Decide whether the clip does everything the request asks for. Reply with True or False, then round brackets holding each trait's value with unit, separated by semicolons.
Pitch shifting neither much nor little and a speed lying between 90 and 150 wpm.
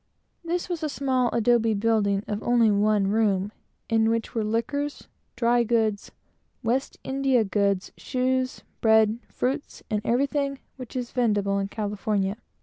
True (3.6 semitones; 140 wpm)